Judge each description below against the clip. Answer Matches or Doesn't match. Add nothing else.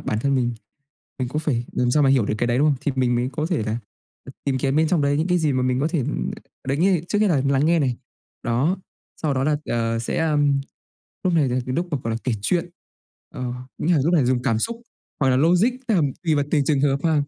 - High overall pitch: Doesn't match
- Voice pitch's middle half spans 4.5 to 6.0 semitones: Doesn't match